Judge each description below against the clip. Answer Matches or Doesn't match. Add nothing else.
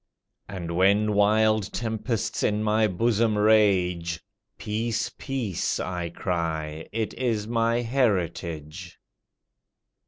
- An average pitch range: Matches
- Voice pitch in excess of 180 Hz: Doesn't match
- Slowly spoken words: Matches